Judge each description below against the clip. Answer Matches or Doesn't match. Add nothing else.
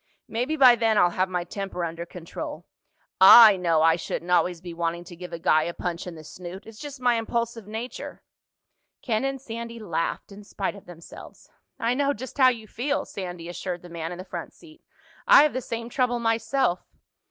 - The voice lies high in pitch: Matches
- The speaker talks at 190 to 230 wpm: Matches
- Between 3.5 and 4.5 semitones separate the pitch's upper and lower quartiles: Doesn't match